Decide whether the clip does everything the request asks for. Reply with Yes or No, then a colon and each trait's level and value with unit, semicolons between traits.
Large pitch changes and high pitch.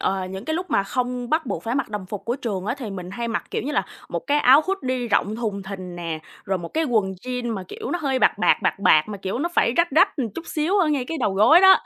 Yes: wide, 7.2 semitones; high, 240 Hz